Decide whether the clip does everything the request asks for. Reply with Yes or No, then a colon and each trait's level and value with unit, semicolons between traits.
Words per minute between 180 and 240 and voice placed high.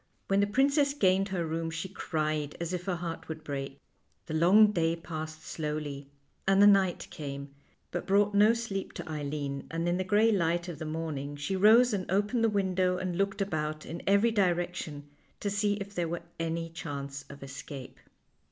No: average, 190 wpm; medium, 175 Hz